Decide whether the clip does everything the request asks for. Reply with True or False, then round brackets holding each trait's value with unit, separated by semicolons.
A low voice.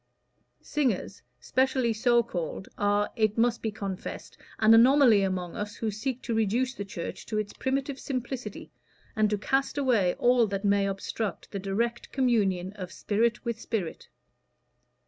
False (220 Hz)